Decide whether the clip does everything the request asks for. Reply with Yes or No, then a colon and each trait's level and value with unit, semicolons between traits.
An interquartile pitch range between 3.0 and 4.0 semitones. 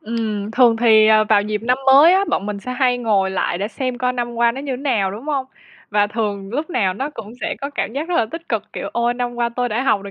Yes: average, 3.4 semitones